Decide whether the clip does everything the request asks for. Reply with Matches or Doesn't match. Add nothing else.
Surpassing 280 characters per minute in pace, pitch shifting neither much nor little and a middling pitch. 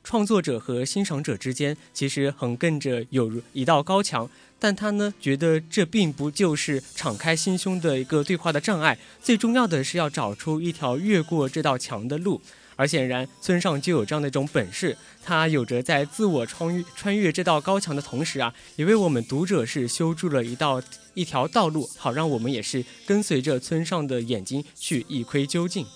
Matches